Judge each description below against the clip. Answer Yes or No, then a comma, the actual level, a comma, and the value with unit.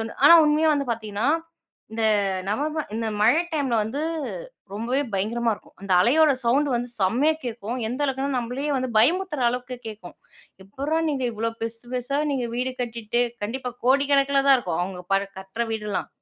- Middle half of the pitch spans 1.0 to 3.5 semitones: No, average, 3.9 semitones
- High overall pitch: Yes, high, 245 Hz